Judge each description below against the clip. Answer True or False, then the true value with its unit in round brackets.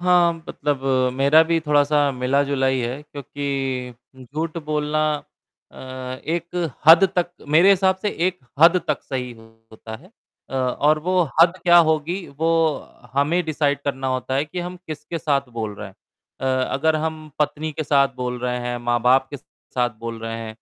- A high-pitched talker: False (145 Hz)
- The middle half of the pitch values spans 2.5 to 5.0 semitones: True (4.0 semitones)